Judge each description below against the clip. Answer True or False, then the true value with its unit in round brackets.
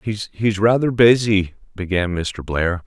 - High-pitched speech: False (100 Hz)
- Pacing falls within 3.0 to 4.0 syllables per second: True (3.9 syllables/s)